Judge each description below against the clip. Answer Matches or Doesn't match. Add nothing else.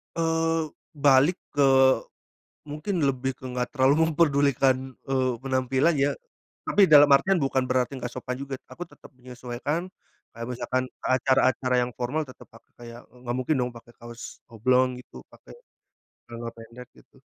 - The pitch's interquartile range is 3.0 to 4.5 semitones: Doesn't match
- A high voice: Doesn't match